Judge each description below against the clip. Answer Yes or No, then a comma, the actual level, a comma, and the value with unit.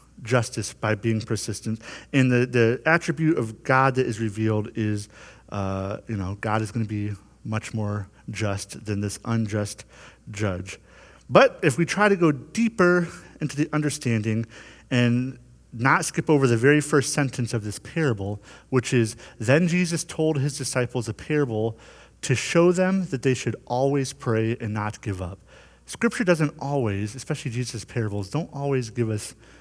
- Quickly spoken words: No, average, 165 wpm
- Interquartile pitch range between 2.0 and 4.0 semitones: No, average, 5.1 semitones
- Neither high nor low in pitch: No, low, 120 Hz